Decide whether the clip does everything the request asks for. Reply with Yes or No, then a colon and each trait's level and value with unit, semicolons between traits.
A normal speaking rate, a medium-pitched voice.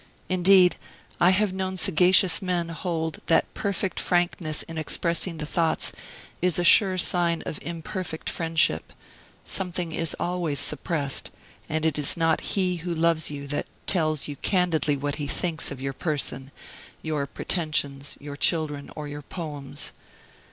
Yes: average, 145 wpm; medium, 165 Hz